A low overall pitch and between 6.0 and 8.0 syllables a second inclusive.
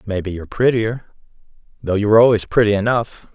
Yes: low, 110 Hz; 6.4 syllables/s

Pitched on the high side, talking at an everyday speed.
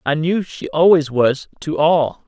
No: medium, 155 Hz; average, 185 wpm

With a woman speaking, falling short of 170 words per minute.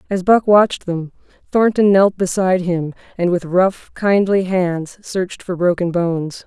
Yes: female; average, 160 wpm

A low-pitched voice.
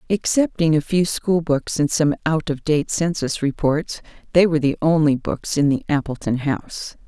No: medium, 155 Hz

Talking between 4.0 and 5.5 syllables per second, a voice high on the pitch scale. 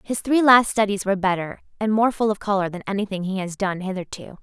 No: 6.1 syllables/s; high, 200 Hz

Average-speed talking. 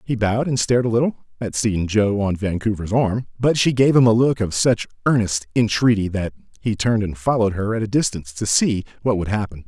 No: fast, 225 wpm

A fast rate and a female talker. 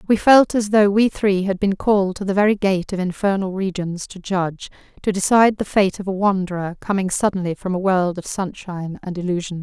Yes: fast, 210 wpm; female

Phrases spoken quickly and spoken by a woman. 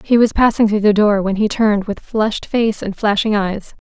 Yes: fast, 230 wpm; female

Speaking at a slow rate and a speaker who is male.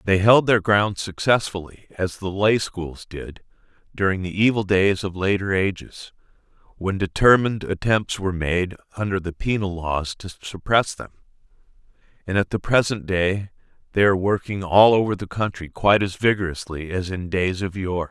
No: average, 155 wpm; male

